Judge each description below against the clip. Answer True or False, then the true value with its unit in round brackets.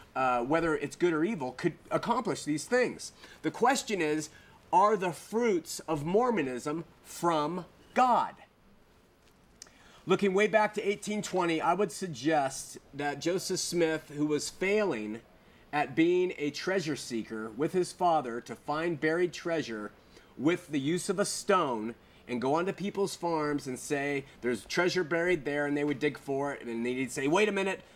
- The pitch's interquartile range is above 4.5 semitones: True (5.2 semitones)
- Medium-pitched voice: True (165 Hz)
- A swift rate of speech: False (165 wpm)